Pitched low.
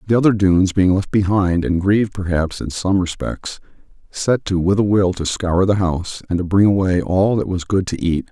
Yes: very low, 95 Hz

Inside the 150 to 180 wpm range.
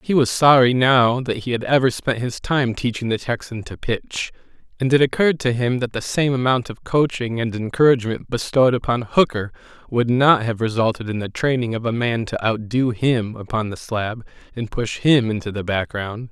No: average, 200 wpm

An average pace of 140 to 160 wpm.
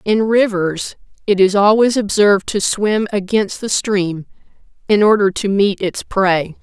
Yes: average, 155 wpm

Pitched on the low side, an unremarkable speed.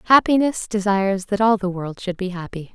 No: high, 200 Hz; average, 195 wpm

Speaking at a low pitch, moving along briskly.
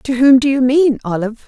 No: very high, 255 Hz; fast, 245 wpm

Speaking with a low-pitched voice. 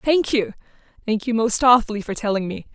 No: high, 225 Hz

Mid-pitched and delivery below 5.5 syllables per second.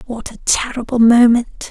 No: high, 235 Hz; 4.5 syllables/s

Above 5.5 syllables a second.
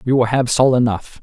No: 5.4 syllables/s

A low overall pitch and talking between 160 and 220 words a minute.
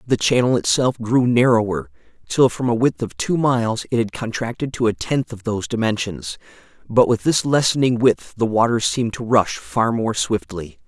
Yes: low, 115 Hz; average, 190 wpm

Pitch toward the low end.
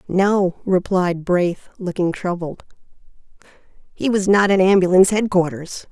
No: medium, 185 Hz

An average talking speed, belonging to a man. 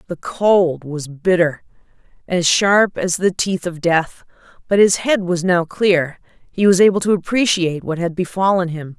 No: average, 175 wpm; female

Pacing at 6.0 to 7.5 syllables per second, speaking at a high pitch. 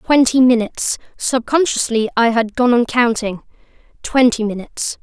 No: 4.9 syllables/s; high, 240 Hz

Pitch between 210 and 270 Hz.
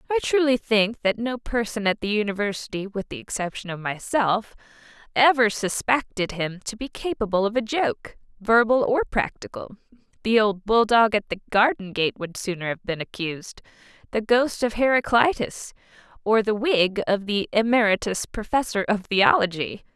Yes: high, 215 Hz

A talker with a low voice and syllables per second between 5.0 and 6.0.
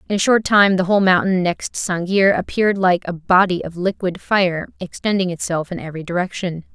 No: medium, 185 Hz; 5.4 syllables/s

